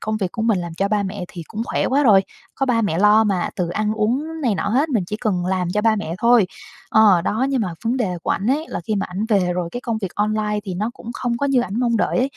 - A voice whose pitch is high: Yes, high, 215 Hz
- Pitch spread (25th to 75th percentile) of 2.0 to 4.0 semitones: Yes, average, 3.7 semitones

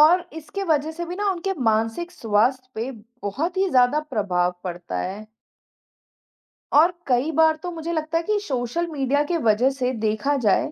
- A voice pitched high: Yes, very high, 280 Hz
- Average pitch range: No, wide, 7.0 semitones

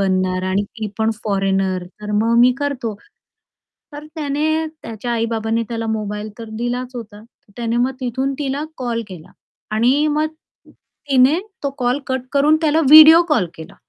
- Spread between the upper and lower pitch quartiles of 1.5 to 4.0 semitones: No, average, 4.7 semitones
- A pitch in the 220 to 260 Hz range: Yes, high, 240 Hz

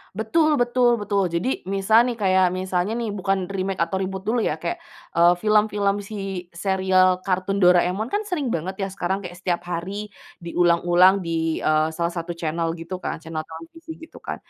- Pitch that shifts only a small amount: No, average, 3.0 semitones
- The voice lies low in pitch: No, high, 190 Hz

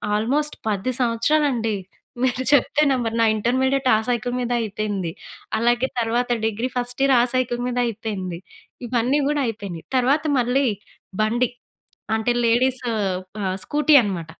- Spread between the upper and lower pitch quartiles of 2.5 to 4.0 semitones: Yes, average, 2.8 semitones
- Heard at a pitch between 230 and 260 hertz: Yes, high, 240 Hz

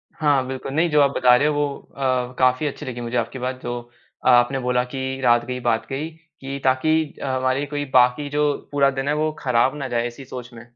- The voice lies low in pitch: Yes, low, 130 Hz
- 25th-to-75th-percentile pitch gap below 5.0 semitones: Yes, narrow, 2.5 semitones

